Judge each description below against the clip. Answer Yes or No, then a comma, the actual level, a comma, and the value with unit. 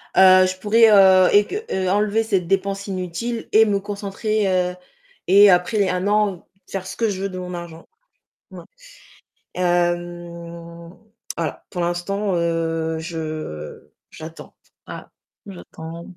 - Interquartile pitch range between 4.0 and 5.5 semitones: No, average, 2.9 semitones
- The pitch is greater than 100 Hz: Yes, medium, 185 Hz